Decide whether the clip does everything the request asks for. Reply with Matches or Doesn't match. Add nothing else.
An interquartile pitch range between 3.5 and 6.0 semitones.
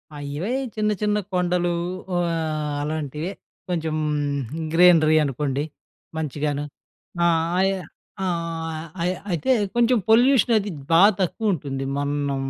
Matches